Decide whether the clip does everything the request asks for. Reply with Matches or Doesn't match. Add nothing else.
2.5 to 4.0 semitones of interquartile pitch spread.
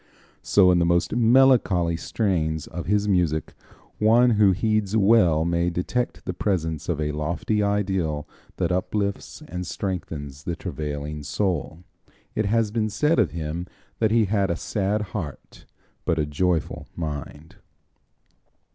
Doesn't match